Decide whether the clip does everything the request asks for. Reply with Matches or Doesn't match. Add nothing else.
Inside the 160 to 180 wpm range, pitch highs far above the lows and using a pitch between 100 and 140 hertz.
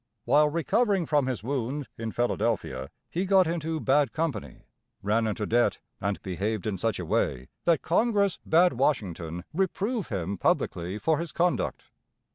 Doesn't match